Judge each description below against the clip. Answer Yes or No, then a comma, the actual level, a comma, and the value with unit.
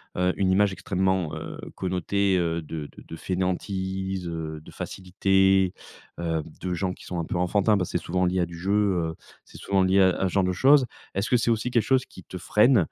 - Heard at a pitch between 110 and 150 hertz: No, very low, 95 Hz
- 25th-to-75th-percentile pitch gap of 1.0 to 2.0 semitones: Yes, narrow, 1.7 semitones